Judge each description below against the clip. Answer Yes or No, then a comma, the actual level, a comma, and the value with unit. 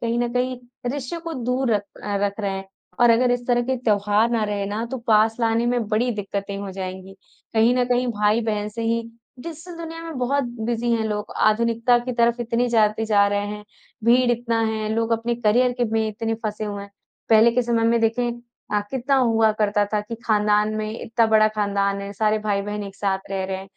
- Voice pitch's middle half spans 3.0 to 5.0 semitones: No, narrow, 2.5 semitones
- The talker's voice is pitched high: Yes, high, 225 Hz